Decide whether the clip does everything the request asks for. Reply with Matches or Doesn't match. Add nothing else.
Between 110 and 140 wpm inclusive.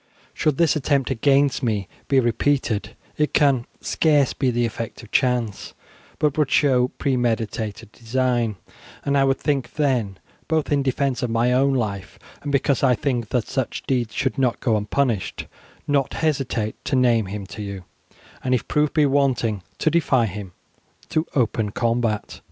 Doesn't match